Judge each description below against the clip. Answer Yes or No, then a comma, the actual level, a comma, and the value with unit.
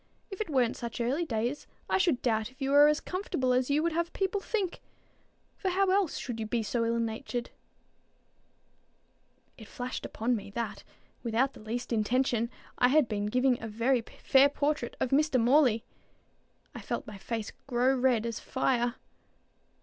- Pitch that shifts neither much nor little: Yes, average, 4.0 semitones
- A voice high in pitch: Yes, very high, 250 Hz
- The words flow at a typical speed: Yes, average, 175 wpm